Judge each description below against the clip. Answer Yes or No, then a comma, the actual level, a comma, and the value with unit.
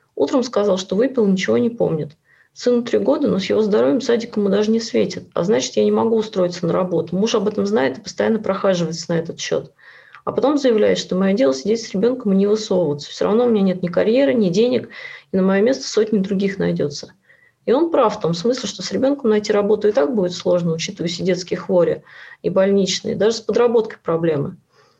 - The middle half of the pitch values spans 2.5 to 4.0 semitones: Yes, average, 3.5 semitones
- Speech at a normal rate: No, fast, 215 wpm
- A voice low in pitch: No, high, 205 Hz